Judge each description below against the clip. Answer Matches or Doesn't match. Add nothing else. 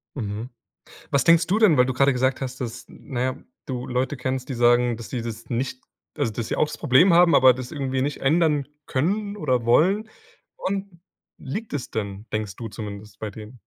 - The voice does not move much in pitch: Doesn't match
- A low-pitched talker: Matches